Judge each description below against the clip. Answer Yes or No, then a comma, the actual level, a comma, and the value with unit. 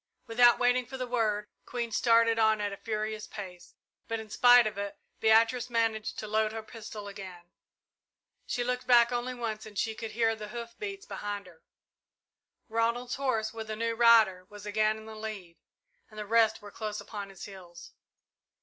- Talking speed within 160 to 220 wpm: Yes, average, 185 wpm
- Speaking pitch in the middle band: No, high, 220 Hz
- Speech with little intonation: Yes, narrow, 2.0 semitones